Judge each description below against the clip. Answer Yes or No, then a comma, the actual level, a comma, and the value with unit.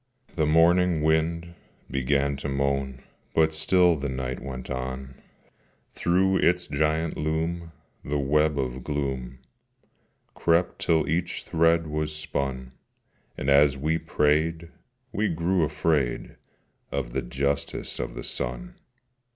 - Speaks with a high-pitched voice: No, very low, 75 Hz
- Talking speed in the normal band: No, slow, 120 wpm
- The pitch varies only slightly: No, average, 3.3 semitones